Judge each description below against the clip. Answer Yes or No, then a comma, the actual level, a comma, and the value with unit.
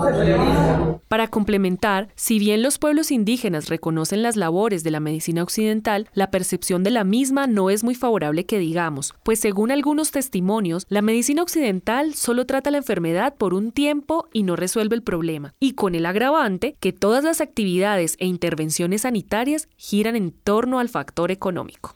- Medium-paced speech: Yes, average, 165 wpm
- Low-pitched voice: No, high, 210 Hz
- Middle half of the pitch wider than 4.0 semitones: Yes, average, 5.3 semitones